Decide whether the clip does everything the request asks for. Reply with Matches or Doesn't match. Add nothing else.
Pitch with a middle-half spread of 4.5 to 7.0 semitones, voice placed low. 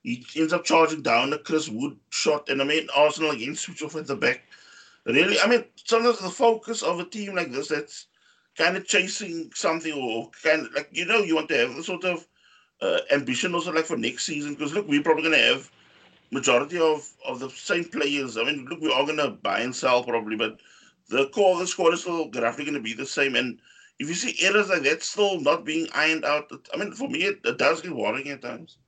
Doesn't match